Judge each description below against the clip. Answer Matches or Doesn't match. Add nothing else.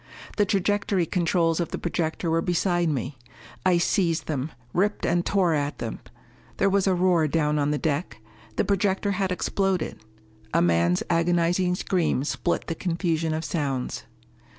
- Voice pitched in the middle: Matches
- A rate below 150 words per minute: Doesn't match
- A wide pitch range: Doesn't match